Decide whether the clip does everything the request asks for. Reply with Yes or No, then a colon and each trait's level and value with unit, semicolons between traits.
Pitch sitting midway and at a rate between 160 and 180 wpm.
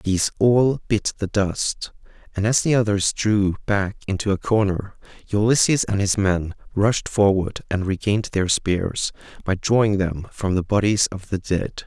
No: low, 100 Hz; average, 165 wpm